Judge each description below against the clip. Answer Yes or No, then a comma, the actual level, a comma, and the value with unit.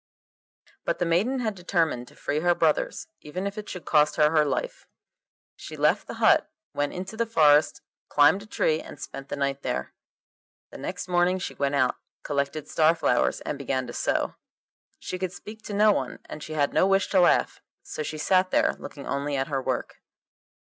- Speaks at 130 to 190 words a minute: No, average, 200 wpm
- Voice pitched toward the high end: No, medium, 160 Hz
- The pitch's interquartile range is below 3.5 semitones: No, average, 4.5 semitones